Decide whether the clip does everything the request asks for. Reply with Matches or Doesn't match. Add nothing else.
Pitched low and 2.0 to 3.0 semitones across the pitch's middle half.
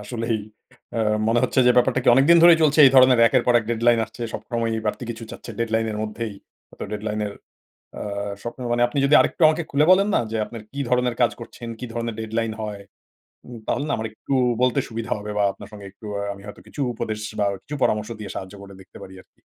Matches